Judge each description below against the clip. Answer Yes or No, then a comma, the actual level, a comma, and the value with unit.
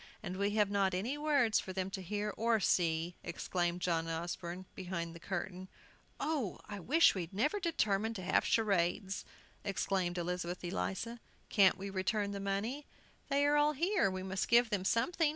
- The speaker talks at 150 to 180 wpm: Yes, average, 170 wpm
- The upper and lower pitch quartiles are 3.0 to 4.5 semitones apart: Yes, average, 4.2 semitones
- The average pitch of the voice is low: No, high, 195 Hz